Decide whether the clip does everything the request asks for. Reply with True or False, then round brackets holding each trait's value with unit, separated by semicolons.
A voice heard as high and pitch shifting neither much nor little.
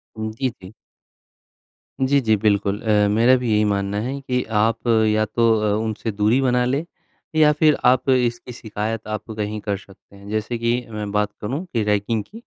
False (110 Hz; 3.0 semitones)